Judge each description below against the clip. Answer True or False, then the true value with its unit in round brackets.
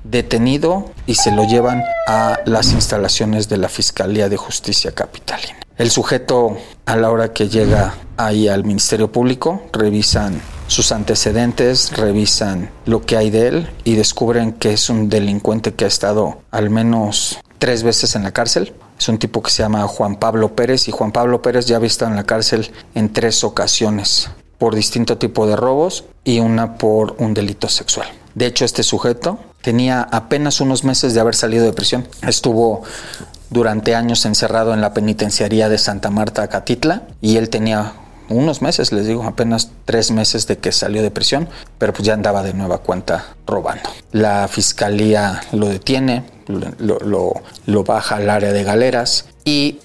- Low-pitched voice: True (110 Hz)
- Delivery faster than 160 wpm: True (170 wpm)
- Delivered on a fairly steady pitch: True (2.0 semitones)